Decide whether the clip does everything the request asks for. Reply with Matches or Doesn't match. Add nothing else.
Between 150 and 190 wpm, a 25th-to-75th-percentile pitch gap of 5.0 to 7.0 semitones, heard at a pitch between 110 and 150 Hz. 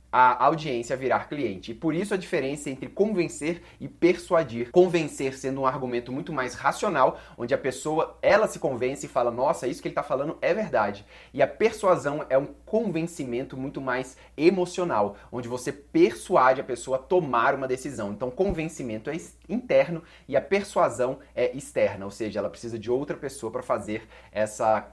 Matches